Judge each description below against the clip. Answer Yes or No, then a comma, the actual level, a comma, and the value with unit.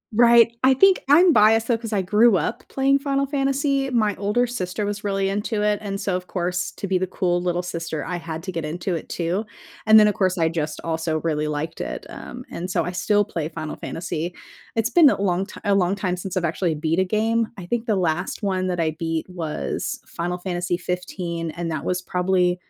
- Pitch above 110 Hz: Yes, medium, 185 Hz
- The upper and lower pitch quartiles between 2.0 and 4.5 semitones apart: Yes, average, 3.9 semitones